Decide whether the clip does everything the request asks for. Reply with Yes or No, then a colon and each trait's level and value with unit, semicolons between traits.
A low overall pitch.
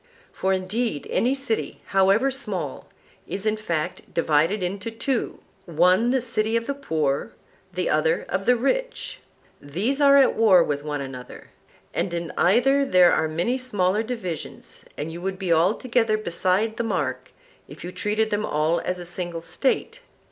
No: high, 190 Hz